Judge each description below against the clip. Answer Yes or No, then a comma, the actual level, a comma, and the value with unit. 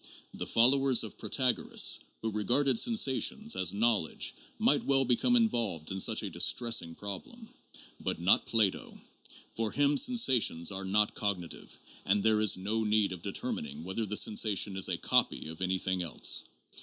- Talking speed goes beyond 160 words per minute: No, average, 155 wpm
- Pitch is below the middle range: Yes, low, 105 Hz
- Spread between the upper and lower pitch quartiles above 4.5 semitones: Yes, average, 5.1 semitones